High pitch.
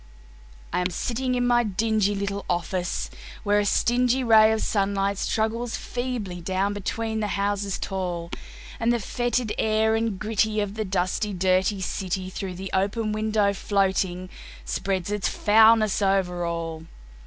Yes: high, 205 Hz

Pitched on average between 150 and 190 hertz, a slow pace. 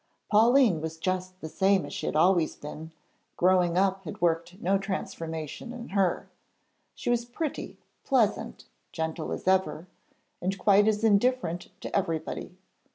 No: medium, 185 Hz; average, 145 wpm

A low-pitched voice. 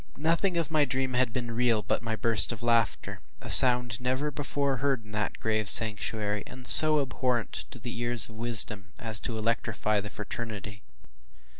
Yes: low, 115 Hz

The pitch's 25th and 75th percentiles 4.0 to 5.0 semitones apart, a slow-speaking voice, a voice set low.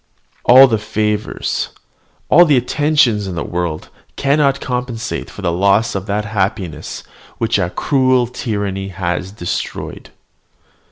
Yes: average, 4.7 semitones; slow, 125 wpm; low, 105 Hz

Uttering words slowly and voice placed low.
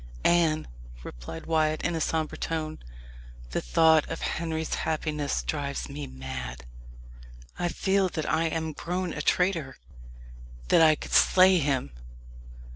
No: slow, 130 wpm; medium, 155 Hz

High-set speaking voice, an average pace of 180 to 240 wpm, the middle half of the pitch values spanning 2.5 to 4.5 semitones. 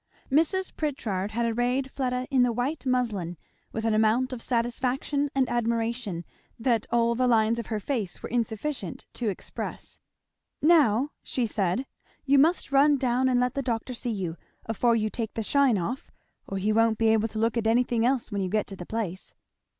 Yes: high, 235 Hz; average, 190 wpm; average, 2.9 semitones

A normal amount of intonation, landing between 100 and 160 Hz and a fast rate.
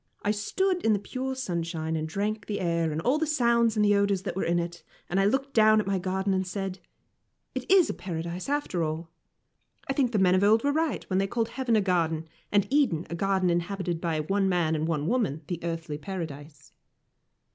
No: average, 4.6 semitones; high, 190 Hz; fast, 215 wpm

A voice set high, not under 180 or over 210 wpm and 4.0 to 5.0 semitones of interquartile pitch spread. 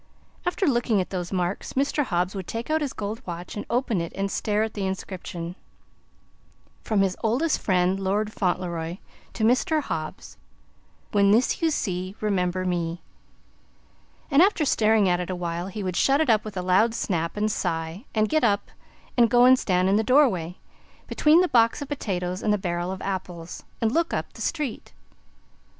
Yes: high, 200 Hz; average, 185 wpm; average, 4.7 semitones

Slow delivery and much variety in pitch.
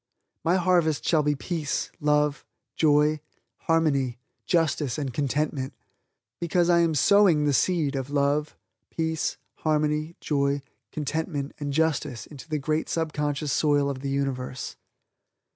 No: slow, 125 wpm; narrow, 2.4 semitones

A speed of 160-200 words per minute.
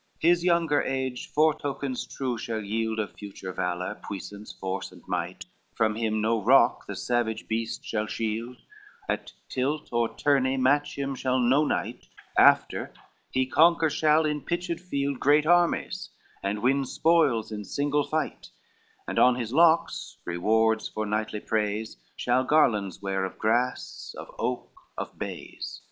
No: average, 150 wpm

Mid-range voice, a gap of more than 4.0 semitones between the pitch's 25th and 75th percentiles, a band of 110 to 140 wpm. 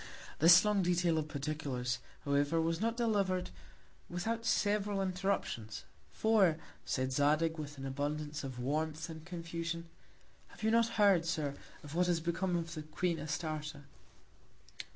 No: medium, 165 Hz; average, 3.7 semitones; slow, 135 wpm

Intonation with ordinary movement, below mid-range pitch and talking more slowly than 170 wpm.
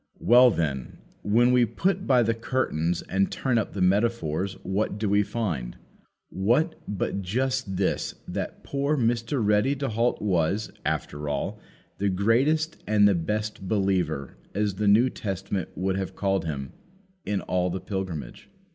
Yes: average, 4.0 semitones; low, 100 Hz; average, 155 wpm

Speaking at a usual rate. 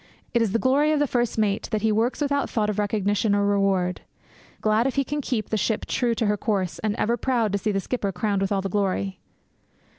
No: fast, 240 wpm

